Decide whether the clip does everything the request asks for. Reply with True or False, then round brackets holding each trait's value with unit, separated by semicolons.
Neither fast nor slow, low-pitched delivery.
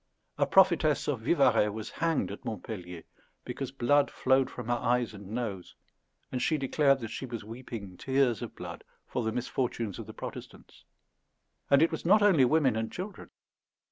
True (170 wpm; 125 Hz)